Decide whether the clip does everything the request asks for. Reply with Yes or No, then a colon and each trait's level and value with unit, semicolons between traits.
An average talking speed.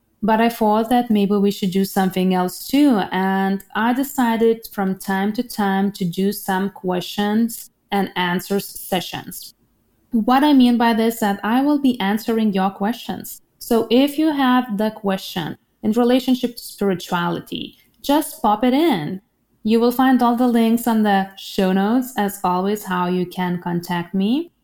Yes: average, 170 wpm